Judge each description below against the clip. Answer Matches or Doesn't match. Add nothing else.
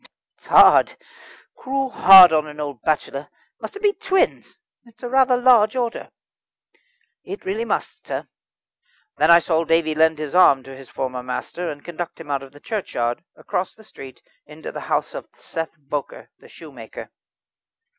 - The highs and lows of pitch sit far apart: Matches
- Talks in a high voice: Doesn't match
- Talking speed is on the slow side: Doesn't match